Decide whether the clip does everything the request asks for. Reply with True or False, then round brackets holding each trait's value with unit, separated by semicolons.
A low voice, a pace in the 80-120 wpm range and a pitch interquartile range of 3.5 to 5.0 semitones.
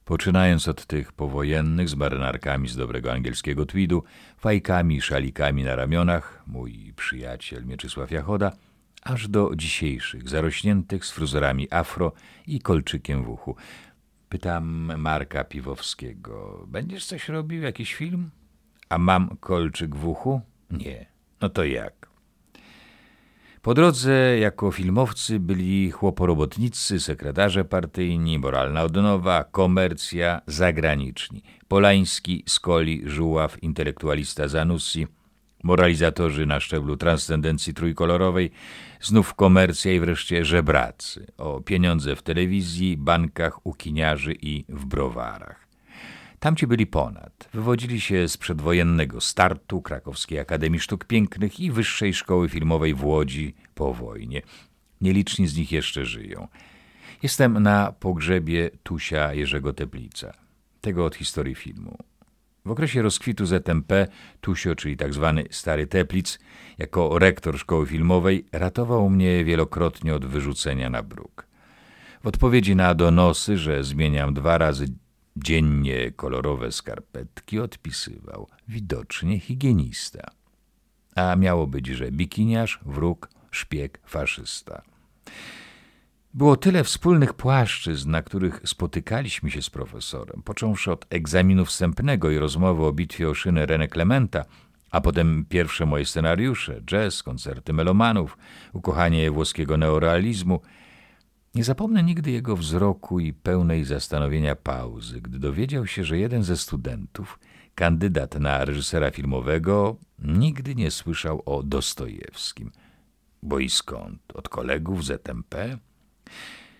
True (85 Hz; 115 wpm; 4.5 semitones)